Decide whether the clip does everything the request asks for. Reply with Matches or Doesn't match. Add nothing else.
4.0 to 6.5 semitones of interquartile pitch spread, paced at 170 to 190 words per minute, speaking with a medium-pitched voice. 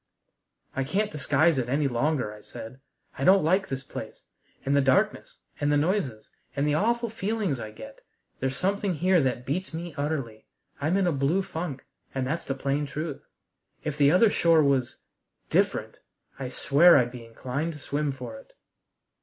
Matches